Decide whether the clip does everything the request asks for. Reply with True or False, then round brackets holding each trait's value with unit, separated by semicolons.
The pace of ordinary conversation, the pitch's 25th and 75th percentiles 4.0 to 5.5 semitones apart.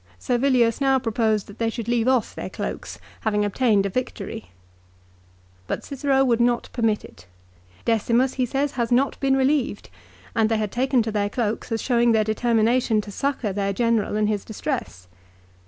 False (170 wpm; 3.1 semitones)